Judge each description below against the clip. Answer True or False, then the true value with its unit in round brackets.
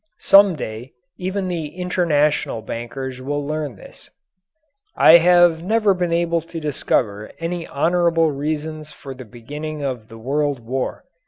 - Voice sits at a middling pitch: True (150 Hz)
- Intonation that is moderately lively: True (4.5 semitones)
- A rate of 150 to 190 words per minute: False (140 wpm)